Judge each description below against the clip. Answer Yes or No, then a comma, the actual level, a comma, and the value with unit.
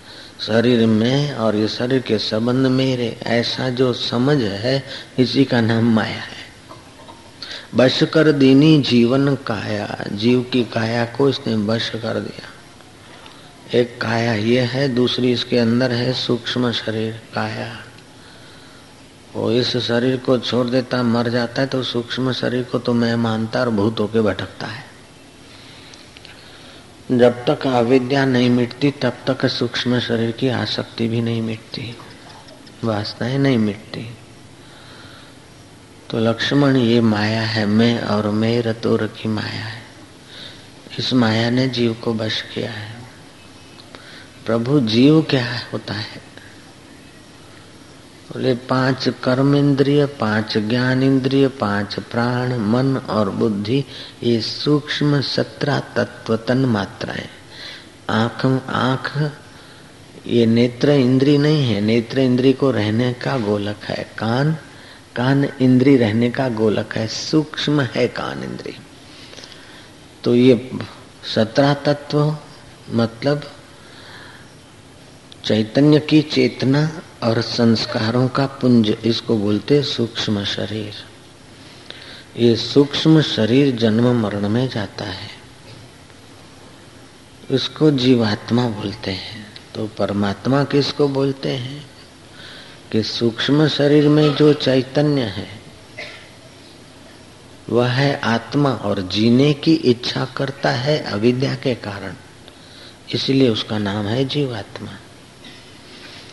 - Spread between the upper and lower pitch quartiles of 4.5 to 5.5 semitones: No, average, 3.2 semitones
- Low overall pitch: Yes, low, 120 Hz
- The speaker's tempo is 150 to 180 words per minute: No, average, 115 wpm